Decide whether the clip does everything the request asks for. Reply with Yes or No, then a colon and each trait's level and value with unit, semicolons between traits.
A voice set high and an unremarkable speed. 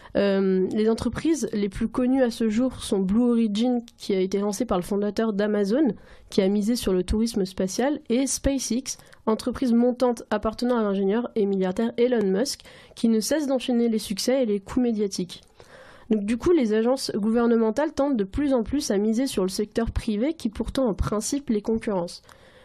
Yes: high, 225 Hz; average, 190 wpm